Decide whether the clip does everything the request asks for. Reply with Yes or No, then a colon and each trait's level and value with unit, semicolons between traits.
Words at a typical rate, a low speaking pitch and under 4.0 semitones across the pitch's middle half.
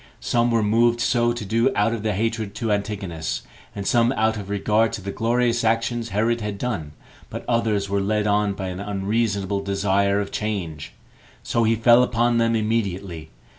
Yes: average, 180 wpm; low, 105 Hz; narrow, 2.6 semitones